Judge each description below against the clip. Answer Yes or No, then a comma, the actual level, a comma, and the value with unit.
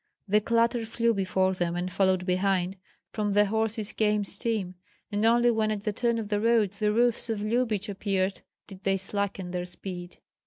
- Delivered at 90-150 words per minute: No, average, 185 wpm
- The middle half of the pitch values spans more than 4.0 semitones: No, average, 2.8 semitones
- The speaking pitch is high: Yes, high, 205 Hz